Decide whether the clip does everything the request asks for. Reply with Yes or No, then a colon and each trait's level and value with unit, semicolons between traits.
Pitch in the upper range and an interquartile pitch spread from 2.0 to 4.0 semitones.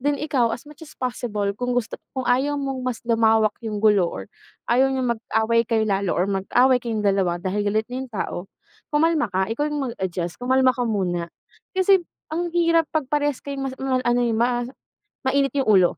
No: high, 245 Hz; average, 4.4 semitones